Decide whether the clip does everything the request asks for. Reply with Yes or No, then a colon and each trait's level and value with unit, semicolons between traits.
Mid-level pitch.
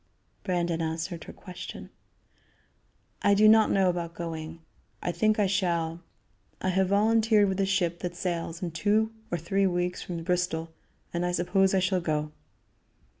Yes: medium, 180 Hz